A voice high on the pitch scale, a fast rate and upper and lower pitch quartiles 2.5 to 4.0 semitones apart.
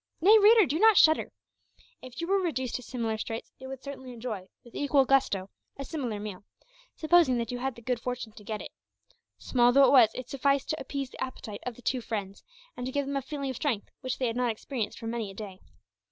Yes: very high, 255 Hz; fast, 235 wpm; average, 3.5 semitones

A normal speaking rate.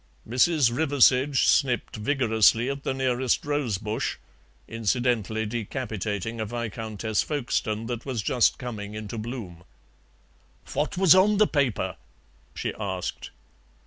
No: slow, 115 wpm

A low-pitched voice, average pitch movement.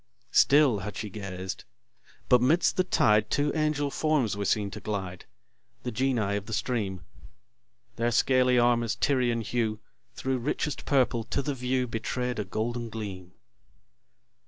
Yes: low, 120 Hz; average, 3.7 semitones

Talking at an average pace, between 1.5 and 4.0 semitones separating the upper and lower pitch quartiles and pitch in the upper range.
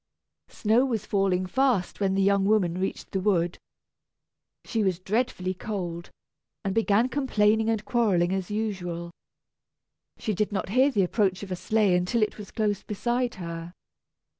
Yes: average, 155 wpm; average, 3.2 semitones; high, 200 Hz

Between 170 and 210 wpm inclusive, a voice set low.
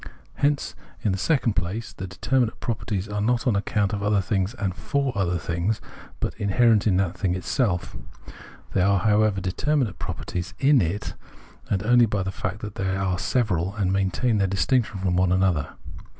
Yes: average, 175 wpm; low, 100 Hz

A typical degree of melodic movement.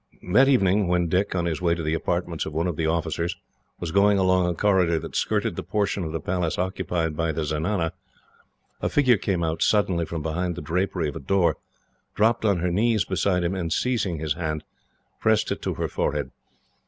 Yes: average, 3.1 semitones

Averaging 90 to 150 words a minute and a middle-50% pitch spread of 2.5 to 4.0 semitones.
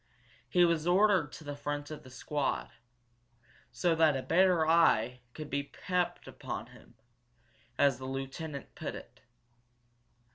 Yes: average, 140 wpm; average, 3.7 semitones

